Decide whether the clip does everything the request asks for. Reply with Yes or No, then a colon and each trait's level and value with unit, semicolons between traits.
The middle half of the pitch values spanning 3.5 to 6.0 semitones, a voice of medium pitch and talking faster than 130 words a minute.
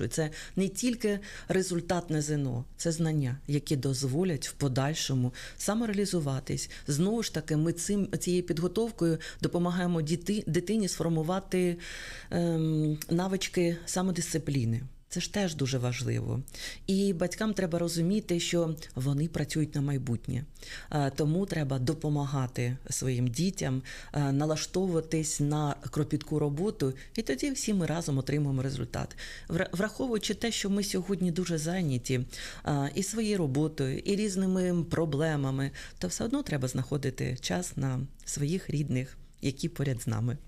No: average, 4.9 semitones; medium, 155 Hz; average, 125 wpm